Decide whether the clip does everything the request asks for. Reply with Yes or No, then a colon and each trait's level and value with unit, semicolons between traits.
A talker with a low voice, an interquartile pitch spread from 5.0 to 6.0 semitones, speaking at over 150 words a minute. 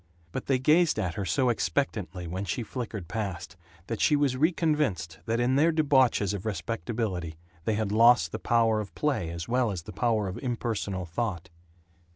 Yes: low, 110 Hz; wide, 5.6 semitones; average, 180 wpm